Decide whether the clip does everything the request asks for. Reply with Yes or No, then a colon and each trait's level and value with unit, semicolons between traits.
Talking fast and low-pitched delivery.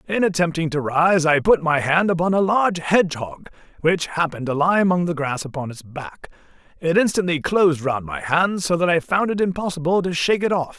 No: fast, 210 wpm; medium, 165 Hz